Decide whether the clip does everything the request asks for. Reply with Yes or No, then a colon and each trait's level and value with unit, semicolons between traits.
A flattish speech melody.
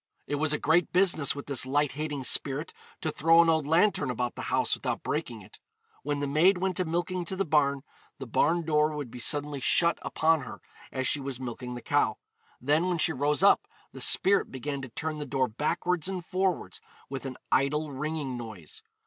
No: average, 3.6 semitones